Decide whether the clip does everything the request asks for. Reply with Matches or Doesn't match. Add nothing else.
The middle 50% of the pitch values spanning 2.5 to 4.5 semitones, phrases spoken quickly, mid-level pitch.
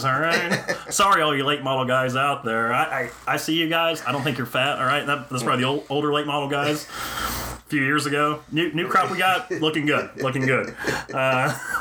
Matches